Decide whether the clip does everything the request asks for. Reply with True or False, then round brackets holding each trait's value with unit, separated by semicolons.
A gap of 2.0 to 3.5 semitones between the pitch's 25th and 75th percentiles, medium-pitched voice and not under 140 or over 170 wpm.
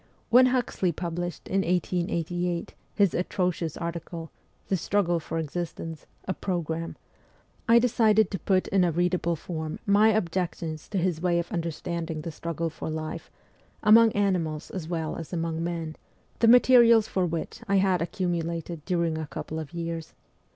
True (2.6 semitones; 175 Hz; 160 wpm)